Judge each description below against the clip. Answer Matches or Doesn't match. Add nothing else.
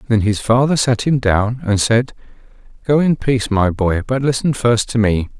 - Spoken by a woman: Doesn't match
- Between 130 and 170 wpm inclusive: Doesn't match